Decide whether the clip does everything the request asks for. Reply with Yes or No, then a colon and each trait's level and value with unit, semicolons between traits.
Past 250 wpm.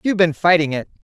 No: fast, 210 wpm